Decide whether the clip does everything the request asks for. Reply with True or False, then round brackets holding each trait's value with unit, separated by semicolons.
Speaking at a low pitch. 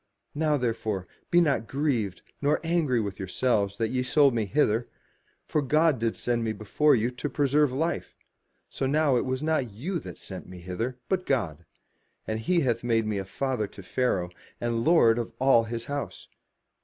True (125 Hz)